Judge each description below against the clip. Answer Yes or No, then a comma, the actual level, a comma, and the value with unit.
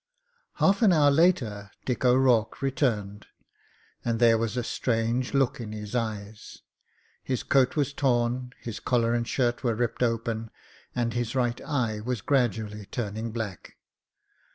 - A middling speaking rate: Yes, average, 145 wpm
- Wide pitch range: No, narrow, 2.5 semitones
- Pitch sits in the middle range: No, low, 120 Hz